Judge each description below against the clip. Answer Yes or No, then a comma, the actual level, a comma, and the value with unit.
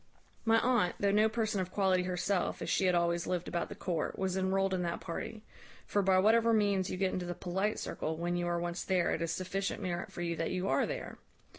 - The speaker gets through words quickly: Yes, fast, 240 wpm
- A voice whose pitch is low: No, medium, 185 Hz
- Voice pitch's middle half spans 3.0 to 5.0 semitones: No, narrow, 2.4 semitones